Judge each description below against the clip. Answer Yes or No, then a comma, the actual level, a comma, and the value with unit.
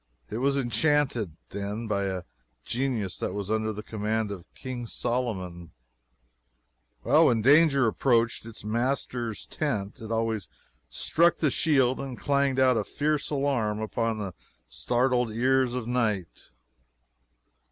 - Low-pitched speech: Yes, low, 115 Hz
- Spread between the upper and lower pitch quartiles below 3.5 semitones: No, average, 3.8 semitones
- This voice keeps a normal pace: No, slow, 130 wpm